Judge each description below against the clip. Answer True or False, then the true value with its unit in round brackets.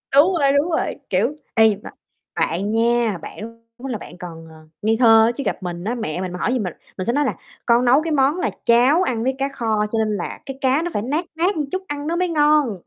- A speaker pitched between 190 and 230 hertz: False (240 Hz)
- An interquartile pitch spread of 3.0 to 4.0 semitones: False (5.2 semitones)